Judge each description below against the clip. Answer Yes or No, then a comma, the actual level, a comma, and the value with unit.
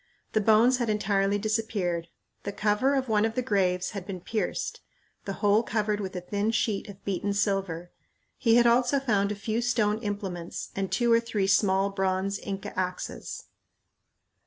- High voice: Yes, high, 205 Hz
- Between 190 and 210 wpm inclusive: No, average, 170 wpm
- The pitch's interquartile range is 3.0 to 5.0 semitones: No, narrow, 2.5 semitones